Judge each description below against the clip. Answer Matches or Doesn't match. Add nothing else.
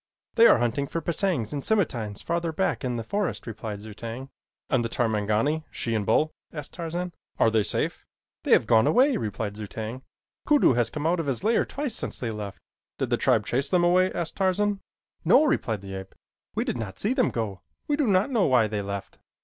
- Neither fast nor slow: Doesn't match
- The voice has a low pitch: Matches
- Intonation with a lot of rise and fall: Matches